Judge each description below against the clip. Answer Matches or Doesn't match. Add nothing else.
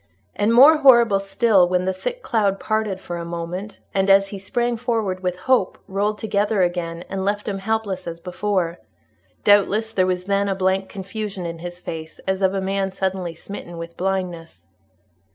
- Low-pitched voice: Doesn't match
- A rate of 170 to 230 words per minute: Matches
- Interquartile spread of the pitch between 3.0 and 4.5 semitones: Doesn't match